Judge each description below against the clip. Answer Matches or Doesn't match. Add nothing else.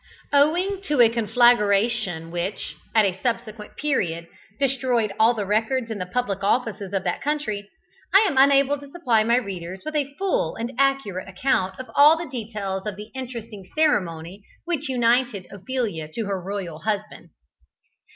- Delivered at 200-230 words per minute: Doesn't match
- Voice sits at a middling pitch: Doesn't match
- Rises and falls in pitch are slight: Doesn't match